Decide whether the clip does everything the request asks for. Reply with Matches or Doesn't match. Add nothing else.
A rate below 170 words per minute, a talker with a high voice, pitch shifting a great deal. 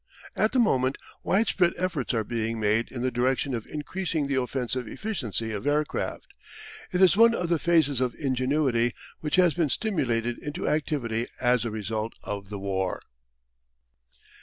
Doesn't match